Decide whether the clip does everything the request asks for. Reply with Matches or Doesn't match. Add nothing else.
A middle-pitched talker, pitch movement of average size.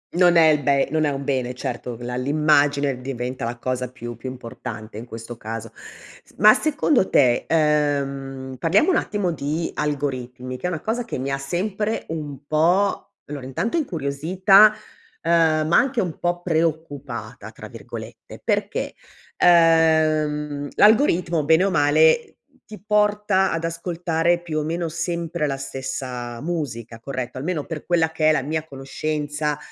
Matches